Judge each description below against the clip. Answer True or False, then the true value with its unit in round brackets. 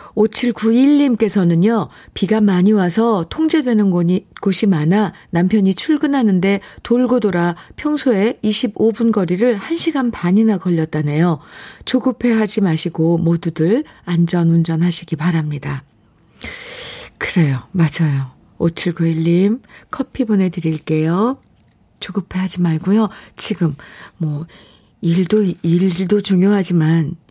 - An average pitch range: True (4.9 semitones)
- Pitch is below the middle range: False (190 Hz)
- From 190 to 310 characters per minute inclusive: True (230 characters per minute)